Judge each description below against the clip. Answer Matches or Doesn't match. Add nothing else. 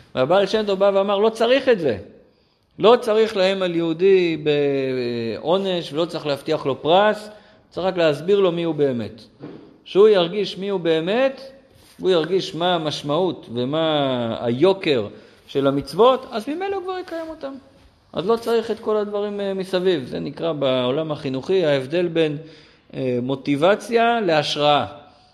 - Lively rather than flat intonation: Matches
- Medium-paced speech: Matches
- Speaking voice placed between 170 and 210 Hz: Matches